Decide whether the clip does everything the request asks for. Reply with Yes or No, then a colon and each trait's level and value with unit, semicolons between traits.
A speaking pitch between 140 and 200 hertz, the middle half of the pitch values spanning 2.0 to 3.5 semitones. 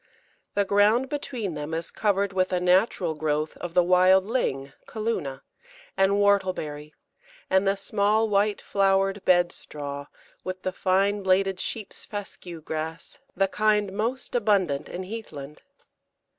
Yes: high, 190 Hz; average, 3.2 semitones